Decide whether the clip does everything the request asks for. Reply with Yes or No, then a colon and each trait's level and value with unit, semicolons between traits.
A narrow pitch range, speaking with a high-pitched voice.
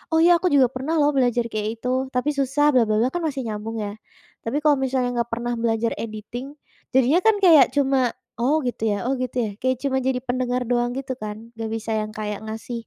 No: average, 3.3 semitones; very high, 250 Hz